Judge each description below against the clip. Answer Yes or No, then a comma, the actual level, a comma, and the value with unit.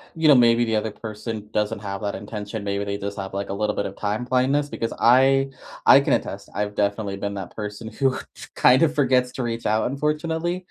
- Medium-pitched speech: No, low, 110 Hz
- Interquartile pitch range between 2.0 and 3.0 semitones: No, average, 4.3 semitones